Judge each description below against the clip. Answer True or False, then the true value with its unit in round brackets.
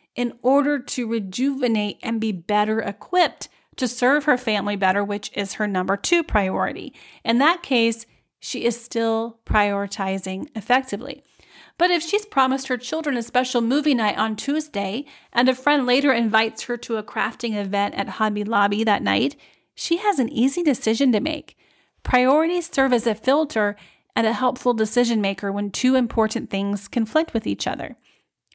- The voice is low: False (235 Hz)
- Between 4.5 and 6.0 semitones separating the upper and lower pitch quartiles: False (4.1 semitones)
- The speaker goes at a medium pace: True (165 wpm)